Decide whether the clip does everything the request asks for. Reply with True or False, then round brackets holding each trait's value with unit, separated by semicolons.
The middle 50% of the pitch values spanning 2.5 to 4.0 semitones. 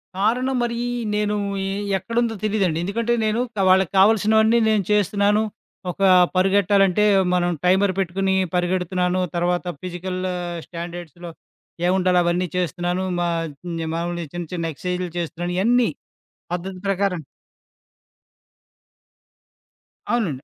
True (2.9 semitones)